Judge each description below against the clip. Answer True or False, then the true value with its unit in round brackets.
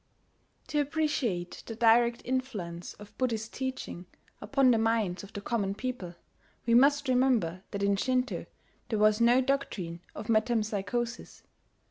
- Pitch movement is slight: False (4.2 semitones)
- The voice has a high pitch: True (230 Hz)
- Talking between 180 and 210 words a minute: False (135 wpm)